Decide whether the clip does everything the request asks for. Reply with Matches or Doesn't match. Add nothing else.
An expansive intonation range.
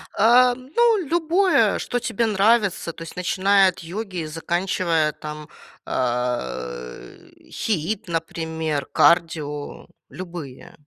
Matches